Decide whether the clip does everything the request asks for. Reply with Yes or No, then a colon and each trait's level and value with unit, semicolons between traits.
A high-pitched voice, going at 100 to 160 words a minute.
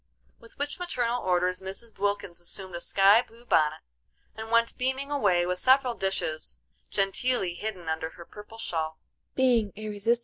Yes: high, 200 Hz; average, 140 wpm